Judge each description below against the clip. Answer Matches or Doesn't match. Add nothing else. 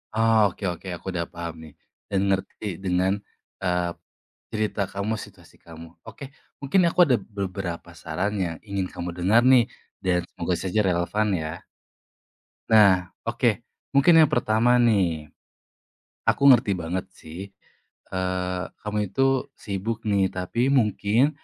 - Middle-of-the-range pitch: Doesn't match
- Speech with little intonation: Doesn't match